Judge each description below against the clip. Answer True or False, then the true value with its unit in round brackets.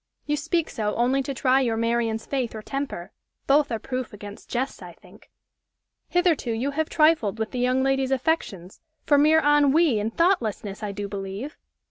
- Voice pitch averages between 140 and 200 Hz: False (255 Hz)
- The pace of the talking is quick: False (175 wpm)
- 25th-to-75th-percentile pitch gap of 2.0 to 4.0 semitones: False (4.8 semitones)